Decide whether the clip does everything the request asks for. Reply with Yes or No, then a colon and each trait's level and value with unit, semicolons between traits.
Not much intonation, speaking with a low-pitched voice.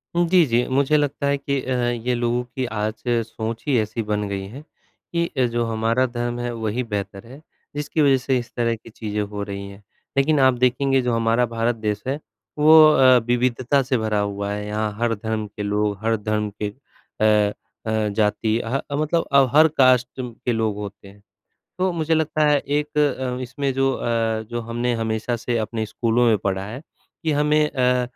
No: average, 3.7 semitones; low, 120 Hz